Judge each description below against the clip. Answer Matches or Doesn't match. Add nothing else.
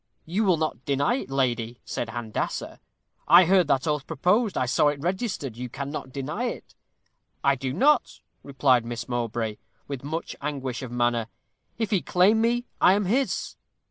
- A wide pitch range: Matches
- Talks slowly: Doesn't match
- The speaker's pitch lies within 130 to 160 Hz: Matches